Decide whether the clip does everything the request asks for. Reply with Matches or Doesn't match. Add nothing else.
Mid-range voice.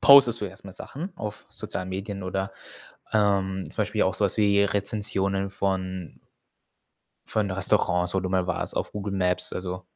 Doesn't match